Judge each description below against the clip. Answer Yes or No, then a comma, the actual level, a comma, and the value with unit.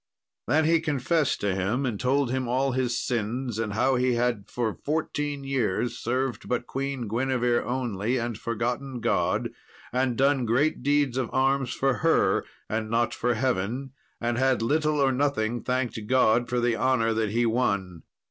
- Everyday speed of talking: Yes, average, 165 wpm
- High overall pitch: No, low, 125 Hz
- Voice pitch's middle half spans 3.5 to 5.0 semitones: No, narrow, 2.5 semitones